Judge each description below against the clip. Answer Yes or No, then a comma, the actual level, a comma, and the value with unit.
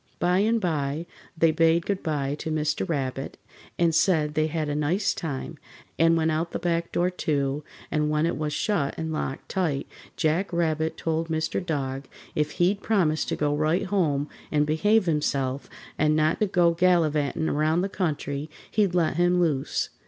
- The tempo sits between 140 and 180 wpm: Yes, average, 170 wpm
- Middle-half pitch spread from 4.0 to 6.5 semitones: No, average, 2.7 semitones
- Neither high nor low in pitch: Yes, medium, 160 Hz